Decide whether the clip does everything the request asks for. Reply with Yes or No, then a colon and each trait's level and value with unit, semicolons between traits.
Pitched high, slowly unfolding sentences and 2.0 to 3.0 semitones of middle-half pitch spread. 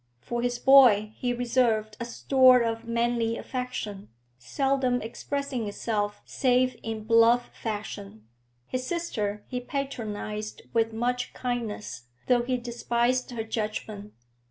Yes: high, 235 Hz; slow, 120 wpm; average, 2.7 semitones